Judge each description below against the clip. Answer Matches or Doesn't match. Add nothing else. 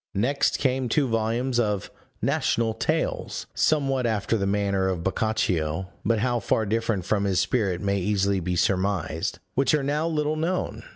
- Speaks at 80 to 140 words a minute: Doesn't match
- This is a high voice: Doesn't match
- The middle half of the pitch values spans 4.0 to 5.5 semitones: Matches